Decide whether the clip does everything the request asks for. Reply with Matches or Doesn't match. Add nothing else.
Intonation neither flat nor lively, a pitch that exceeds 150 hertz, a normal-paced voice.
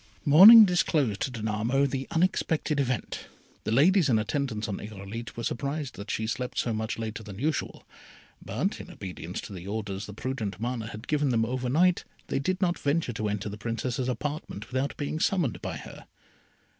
Doesn't match